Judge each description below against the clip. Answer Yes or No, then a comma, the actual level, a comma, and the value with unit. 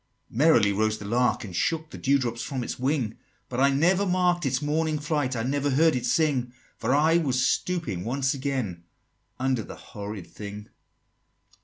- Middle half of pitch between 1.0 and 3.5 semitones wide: No, average, 5.2 semitones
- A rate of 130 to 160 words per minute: No, average, 180 wpm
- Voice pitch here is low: Yes, low, 130 Hz